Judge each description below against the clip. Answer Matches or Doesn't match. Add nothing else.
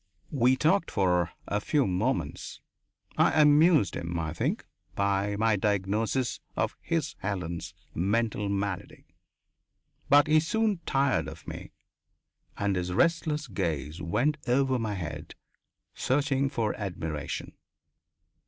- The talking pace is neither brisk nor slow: Doesn't match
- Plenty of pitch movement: Matches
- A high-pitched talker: Doesn't match